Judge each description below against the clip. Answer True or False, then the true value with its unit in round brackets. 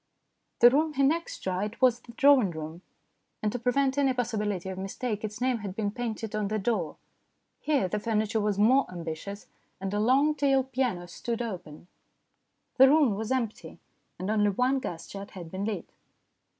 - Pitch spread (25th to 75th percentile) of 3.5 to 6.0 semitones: True (4.6 semitones)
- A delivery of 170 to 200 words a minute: True (175 wpm)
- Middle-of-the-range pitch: False (220 Hz)